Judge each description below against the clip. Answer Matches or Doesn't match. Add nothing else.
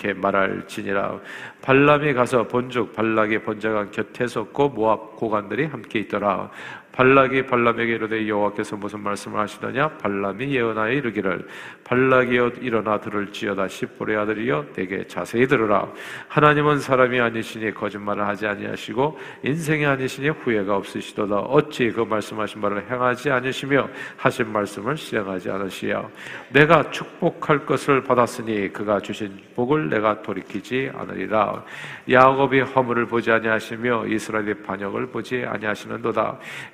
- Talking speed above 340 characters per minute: Matches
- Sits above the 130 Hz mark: Doesn't match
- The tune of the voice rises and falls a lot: Doesn't match